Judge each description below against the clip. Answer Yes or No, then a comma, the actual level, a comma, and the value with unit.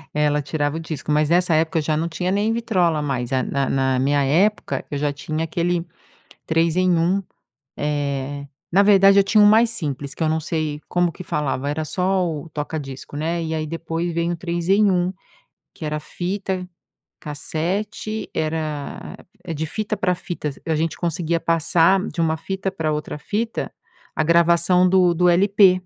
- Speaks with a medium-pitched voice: Yes, medium, 165 Hz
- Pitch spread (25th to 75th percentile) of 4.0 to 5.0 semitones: No, average, 3.5 semitones